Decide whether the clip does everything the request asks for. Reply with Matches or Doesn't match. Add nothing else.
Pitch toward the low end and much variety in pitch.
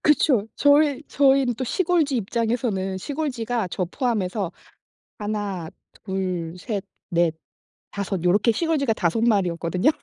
Doesn't match